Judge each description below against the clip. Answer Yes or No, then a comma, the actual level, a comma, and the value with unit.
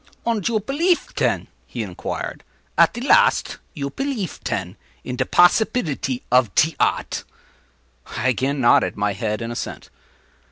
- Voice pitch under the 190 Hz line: Yes, medium, 140 Hz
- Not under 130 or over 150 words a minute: Yes, average, 145 wpm